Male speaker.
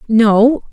No: female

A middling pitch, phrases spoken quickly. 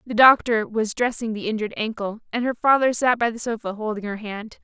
No: high, 225 Hz; fast, 220 wpm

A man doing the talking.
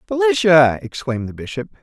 Yes: male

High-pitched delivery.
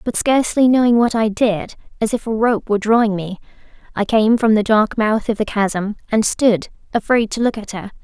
Yes: high, 220 Hz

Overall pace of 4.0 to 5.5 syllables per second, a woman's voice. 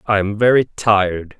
No: 4.8 syllables/s; male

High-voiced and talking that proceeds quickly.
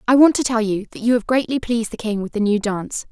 Yes: high, 225 Hz; fast, 310 wpm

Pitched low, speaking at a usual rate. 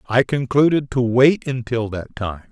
Yes: low, 125 Hz; average, 165 wpm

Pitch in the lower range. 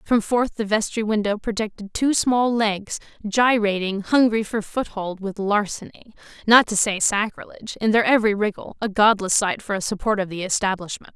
No: high, 210 Hz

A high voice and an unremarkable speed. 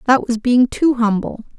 Yes: high, 240 Hz; average, 190 wpm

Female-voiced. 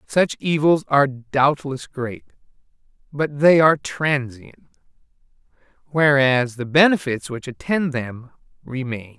No: male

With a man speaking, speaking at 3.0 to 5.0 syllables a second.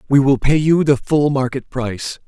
Yes: male; 4.9 syllables/s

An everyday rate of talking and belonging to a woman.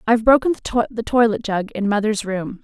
Yes: average, 180 wpm; female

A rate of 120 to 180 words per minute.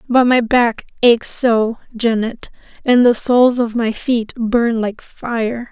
Yes: average, 155 wpm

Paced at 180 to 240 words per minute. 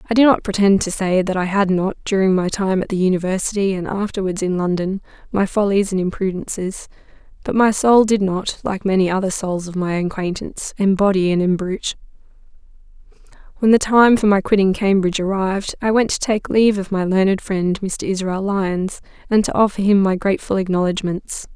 Yes: average, 185 wpm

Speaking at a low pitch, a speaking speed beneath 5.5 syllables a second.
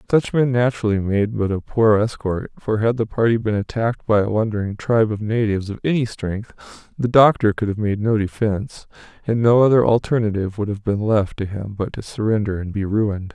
No: low, 110 Hz; 5.6 syllables/s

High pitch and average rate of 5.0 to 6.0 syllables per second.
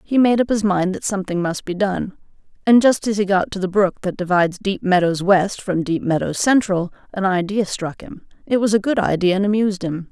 Yes: high, 195 Hz; 5.5 syllables/s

